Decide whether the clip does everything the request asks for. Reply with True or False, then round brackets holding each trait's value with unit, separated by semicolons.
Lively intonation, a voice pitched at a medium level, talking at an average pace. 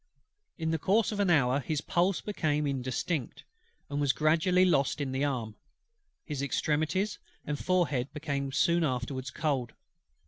False (3.9 semitones; 150 Hz; 145 wpm)